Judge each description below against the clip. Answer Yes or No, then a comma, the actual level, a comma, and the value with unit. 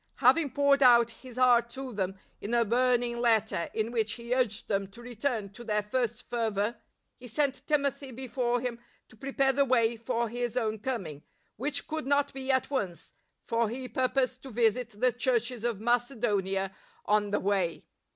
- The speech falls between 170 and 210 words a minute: Yes, average, 175 wpm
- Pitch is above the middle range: Yes, high, 240 Hz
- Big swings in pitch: No, average, 2.9 semitones